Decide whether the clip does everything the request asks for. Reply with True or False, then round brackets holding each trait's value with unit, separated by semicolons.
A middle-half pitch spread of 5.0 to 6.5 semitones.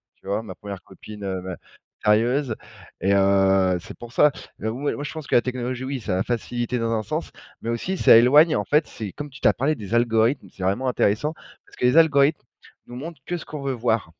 True (5.3 semitones)